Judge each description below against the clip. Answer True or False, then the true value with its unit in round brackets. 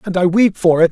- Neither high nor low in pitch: True (180 Hz)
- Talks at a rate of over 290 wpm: True (330 wpm)